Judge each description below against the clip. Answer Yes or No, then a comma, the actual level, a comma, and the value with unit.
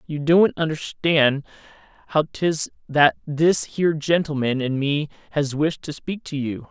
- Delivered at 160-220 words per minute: No, average, 150 wpm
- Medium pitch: Yes, medium, 150 Hz